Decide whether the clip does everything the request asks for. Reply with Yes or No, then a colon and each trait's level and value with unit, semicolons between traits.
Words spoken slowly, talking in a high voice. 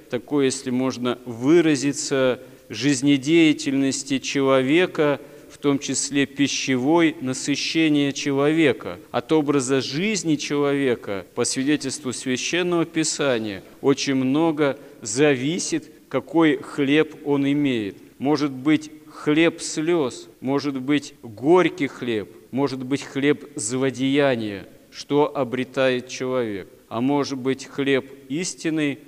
No: slow, 95 wpm; medium, 140 Hz